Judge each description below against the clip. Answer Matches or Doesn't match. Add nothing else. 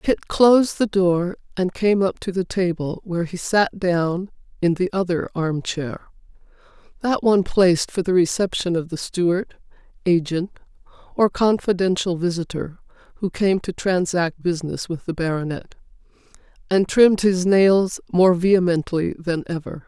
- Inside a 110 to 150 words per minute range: Matches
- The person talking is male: Doesn't match